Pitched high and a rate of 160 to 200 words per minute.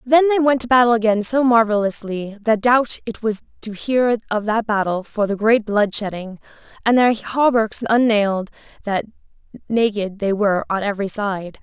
Yes: high, 220 Hz; average, 170 wpm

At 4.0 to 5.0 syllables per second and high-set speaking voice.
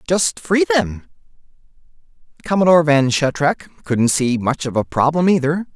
No: 4.7 syllables/s; medium, 150 Hz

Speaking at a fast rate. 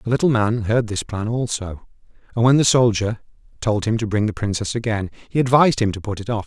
Yes: fast, 230 wpm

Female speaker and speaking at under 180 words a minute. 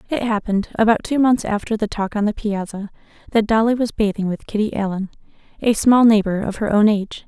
No: female; fast, 205 wpm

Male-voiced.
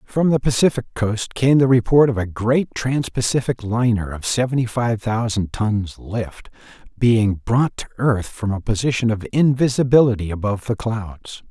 Yes: male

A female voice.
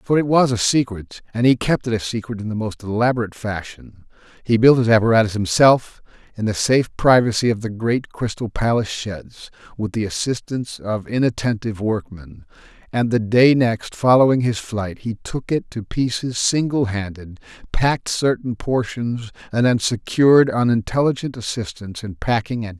No: male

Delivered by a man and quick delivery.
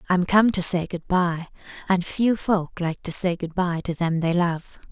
No: female; fast, 220 wpm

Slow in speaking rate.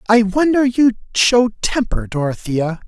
Yes: slow, 125 wpm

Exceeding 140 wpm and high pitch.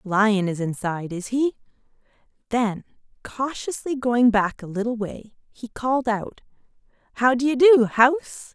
No: slow, 135 wpm; high, 235 Hz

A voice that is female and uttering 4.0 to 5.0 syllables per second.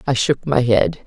Yes: female; 4.7 syllables/s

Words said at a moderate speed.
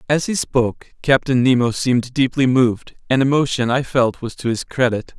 Yes: average, 185 wpm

